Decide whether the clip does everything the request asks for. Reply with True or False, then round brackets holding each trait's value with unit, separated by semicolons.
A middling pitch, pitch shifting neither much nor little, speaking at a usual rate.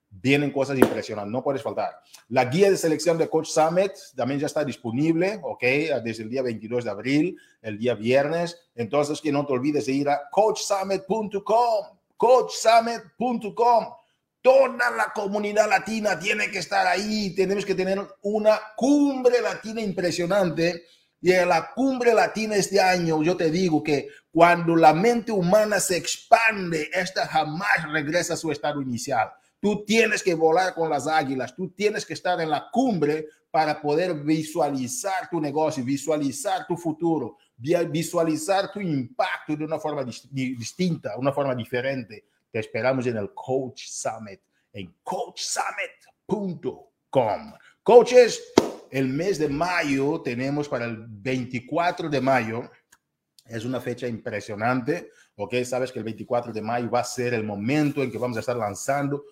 False (160 Hz; 6.8 semitones; 150 wpm)